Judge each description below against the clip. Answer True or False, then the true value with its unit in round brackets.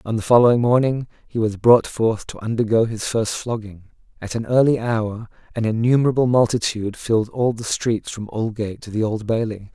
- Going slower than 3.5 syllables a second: False (5.4 syllables/s)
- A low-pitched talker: True (115 Hz)